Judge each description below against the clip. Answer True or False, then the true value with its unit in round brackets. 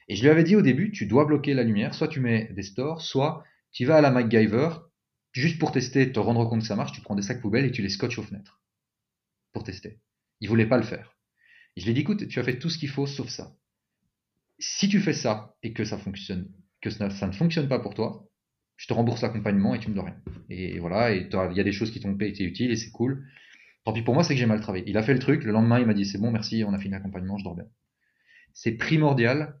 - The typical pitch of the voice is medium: False (115 Hz)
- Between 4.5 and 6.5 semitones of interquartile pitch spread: True (5.0 semitones)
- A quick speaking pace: True (280 wpm)